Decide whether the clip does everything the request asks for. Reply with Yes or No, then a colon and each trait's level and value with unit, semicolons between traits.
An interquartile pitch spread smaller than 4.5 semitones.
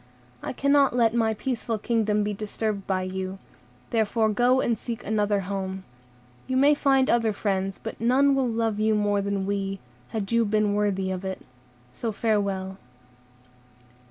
Yes: average, 2.8 semitones